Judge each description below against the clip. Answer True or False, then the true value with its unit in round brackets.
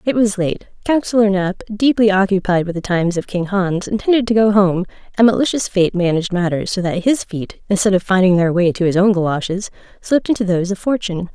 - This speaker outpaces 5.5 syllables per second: True (6.0 syllables/s)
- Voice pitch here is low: False (195 Hz)